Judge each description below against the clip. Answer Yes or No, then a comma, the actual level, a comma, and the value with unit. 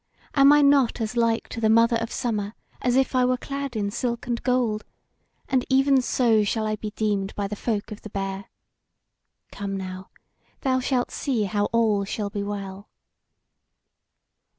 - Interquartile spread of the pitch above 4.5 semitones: No, average, 3.6 semitones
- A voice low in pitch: No, high, 225 Hz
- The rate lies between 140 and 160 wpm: No, average, 175 wpm